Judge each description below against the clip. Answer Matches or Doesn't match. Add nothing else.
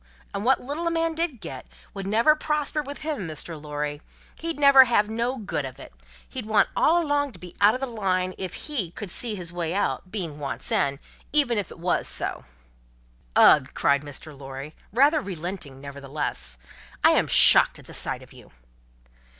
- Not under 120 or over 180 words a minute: Doesn't match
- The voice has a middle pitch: Doesn't match